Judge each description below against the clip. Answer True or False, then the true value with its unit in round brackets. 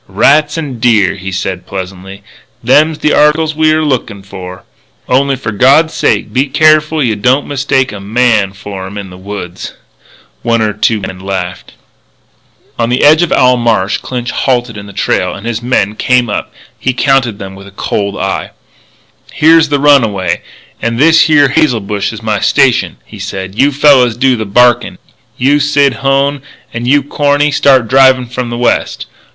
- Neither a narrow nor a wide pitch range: False (5.8 semitones)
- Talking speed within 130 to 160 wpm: False (175 wpm)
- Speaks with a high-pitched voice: False (120 Hz)